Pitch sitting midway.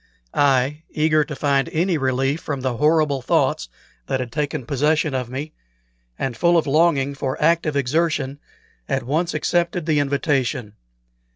Yes: medium, 145 Hz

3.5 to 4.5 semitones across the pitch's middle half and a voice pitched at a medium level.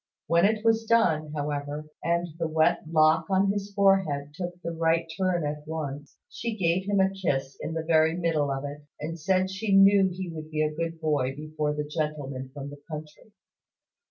Yes: average, 4.0 semitones; medium, 160 Hz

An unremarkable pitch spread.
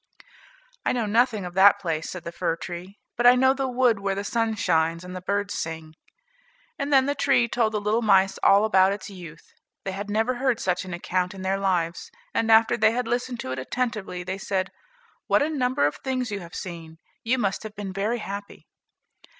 Yes: average, 4.5 semitones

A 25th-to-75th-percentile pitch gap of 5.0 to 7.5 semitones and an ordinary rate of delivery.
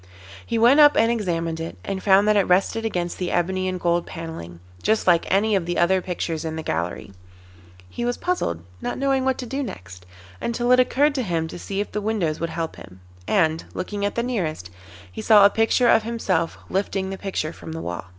No: average, 5.3 semitones; fast, 220 wpm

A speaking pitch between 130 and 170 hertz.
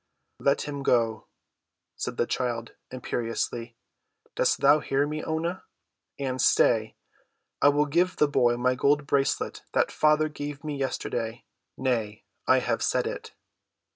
Yes: low, 135 Hz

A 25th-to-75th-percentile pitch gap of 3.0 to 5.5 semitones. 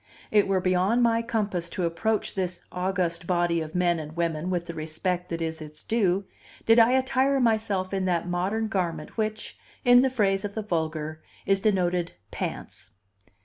Yes: average, 4.2 semitones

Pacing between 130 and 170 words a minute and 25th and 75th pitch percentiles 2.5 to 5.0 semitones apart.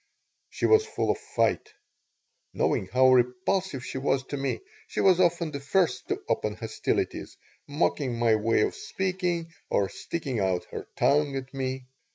No: average, 160 wpm; wide, 5.4 semitones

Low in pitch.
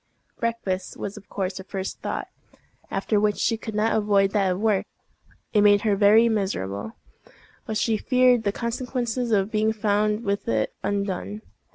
No: high, 210 Hz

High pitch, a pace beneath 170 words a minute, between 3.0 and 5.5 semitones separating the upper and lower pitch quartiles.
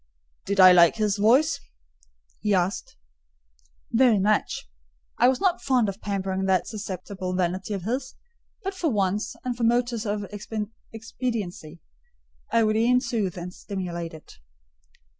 Yes: high, 210 Hz; average, 140 wpm; average, 4.1 semitones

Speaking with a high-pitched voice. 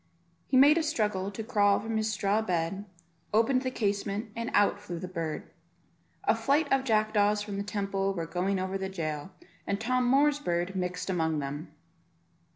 Yes: high, 200 Hz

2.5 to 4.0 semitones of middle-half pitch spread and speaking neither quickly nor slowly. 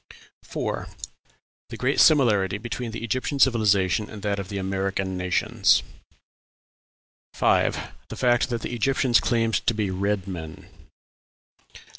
No: average, 3.7 semitones; slow, 125 wpm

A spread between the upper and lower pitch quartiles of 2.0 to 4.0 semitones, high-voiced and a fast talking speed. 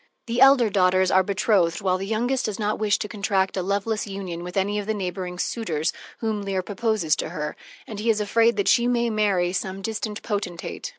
Yes: average, 2.8 semitones; high, 200 Hz; fast, 210 wpm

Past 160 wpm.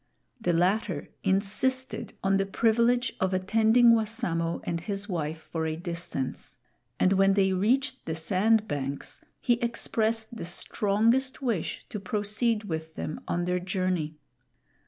No: slow, 135 wpm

